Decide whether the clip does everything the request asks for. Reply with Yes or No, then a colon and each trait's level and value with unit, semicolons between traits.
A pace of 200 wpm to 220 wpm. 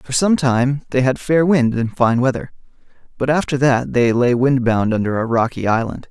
Yes: fast, 205 wpm